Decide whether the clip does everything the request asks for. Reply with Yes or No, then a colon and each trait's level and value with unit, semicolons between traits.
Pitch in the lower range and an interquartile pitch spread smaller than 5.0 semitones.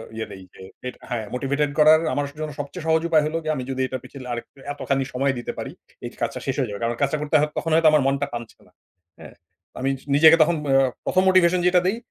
No: medium, 145 Hz; average, 3.4 semitones